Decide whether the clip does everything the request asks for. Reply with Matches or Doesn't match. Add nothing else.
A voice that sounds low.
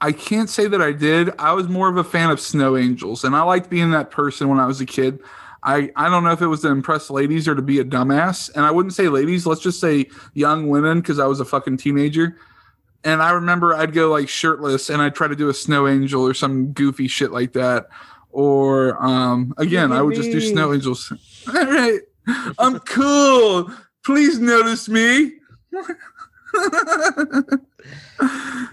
Doesn't match